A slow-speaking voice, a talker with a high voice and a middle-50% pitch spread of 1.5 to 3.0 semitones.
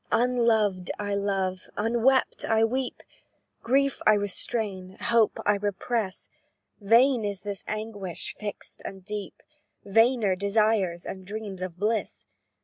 Yes: slow, 120 wpm; high, 210 Hz; average, 2.7 semitones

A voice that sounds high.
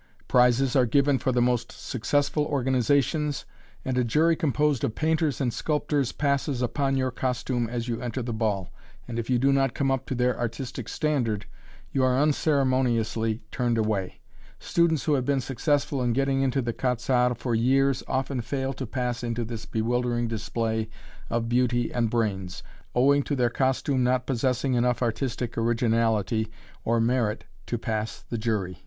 No: low, 125 Hz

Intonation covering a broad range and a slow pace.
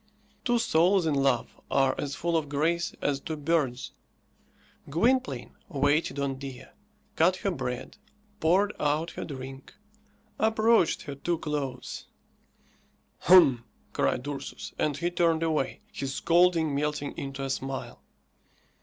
No: average, 3.9 semitones; slow, 125 wpm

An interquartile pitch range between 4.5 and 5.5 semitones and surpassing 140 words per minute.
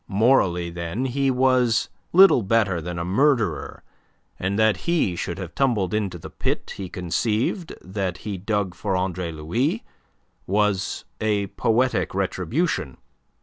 No: average, 5.0 semitones; slow, 135 wpm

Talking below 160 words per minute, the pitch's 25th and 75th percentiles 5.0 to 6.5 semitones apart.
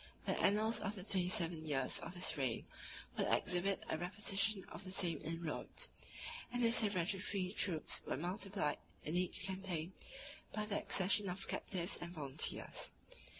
No: average, 150 wpm; average, 3.2 semitones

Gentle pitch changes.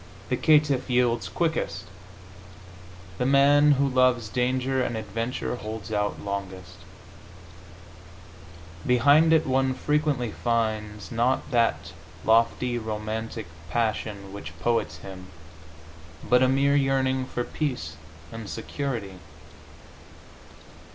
No: average, 3.7 semitones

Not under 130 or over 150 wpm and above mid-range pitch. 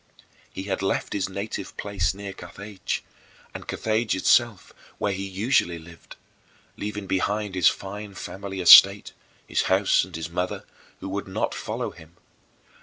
No: average, 145 wpm; very low, 95 Hz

